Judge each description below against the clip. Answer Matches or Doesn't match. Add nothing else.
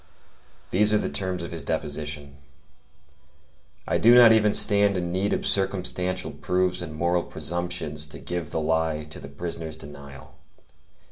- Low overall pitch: Matches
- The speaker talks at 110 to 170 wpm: Matches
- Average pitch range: Matches